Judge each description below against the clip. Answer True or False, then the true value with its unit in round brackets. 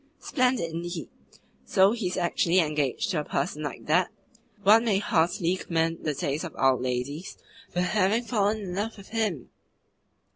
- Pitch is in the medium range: True (180 Hz)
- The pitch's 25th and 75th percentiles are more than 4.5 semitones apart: True (4.9 semitones)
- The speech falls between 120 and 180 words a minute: True (160 wpm)